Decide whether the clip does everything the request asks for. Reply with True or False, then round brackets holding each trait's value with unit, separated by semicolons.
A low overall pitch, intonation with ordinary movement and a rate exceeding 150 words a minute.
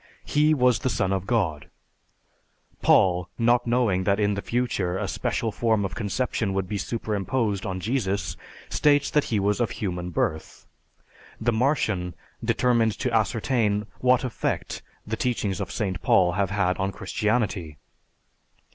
False (105 Hz; 4.0 semitones; 145 wpm)